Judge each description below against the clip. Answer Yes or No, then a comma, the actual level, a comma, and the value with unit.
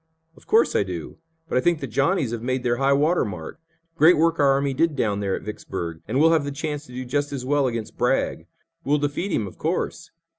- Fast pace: Yes, fast, 235 wpm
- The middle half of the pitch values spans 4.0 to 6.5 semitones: Yes, average, 4.6 semitones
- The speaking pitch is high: No, medium, 140 Hz